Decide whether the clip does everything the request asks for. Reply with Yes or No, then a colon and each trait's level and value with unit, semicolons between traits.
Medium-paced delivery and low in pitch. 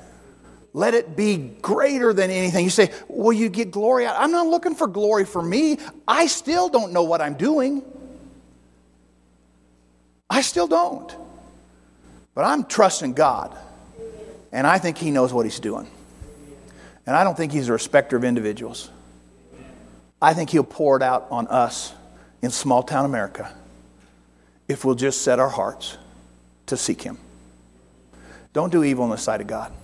Yes: average, 160 wpm; low, 130 Hz